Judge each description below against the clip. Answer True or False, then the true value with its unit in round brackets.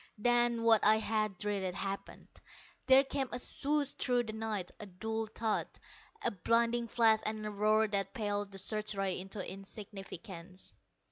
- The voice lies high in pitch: True (215 Hz)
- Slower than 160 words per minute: True (150 wpm)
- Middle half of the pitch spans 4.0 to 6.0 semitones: False (2.8 semitones)